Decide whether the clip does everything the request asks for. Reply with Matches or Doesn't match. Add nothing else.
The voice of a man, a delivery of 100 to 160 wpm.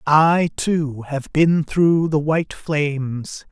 Matches